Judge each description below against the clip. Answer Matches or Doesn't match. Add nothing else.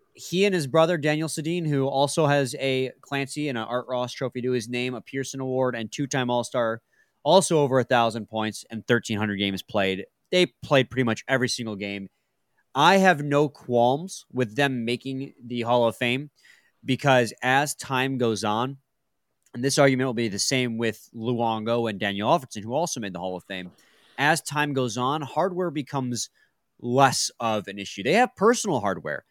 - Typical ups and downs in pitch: Matches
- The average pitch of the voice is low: Matches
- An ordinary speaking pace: Matches